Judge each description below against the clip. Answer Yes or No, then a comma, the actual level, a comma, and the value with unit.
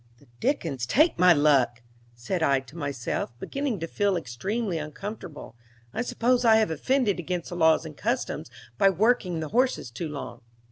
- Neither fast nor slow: Yes, average, 170 wpm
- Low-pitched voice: No, medium, 170 Hz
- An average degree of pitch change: No, wide, 7.6 semitones